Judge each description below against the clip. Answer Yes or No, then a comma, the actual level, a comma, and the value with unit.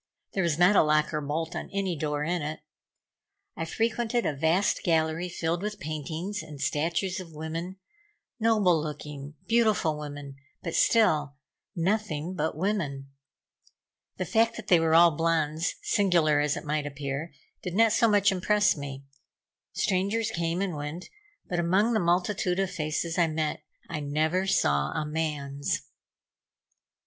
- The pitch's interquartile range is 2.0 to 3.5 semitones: No, average, 4.1 semitones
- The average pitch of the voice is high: No, medium, 165 Hz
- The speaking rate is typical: Yes, average, 150 wpm